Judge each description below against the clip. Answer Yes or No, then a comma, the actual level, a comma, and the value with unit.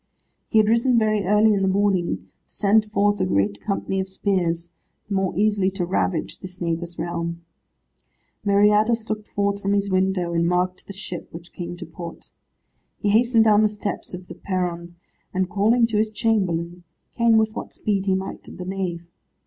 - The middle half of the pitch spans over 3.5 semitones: No, average, 3.1 semitones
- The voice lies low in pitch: No, high, 195 Hz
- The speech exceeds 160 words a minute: Yes, average, 185 wpm